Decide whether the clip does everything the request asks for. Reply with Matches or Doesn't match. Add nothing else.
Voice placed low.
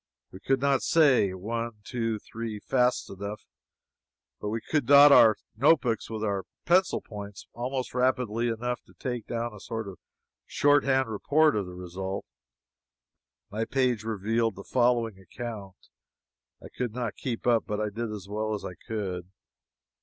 Matches